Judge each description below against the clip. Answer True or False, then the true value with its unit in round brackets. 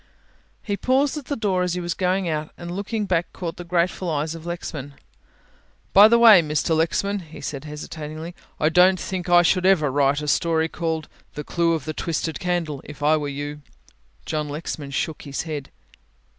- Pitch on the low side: False (165 Hz)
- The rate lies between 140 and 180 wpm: False (190 wpm)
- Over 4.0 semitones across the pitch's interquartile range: False (3.2 semitones)